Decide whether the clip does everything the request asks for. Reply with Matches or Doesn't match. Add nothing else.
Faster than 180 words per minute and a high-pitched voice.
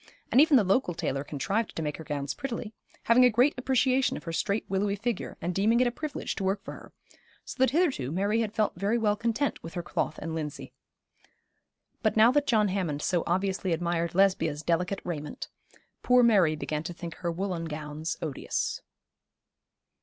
Matches